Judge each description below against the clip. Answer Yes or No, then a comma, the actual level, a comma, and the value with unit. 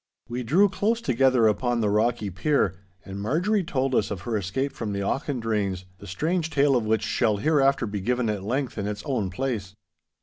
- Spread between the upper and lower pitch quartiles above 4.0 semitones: Yes, average, 5.0 semitones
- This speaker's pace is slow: No, average, 195 wpm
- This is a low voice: Yes, low, 120 Hz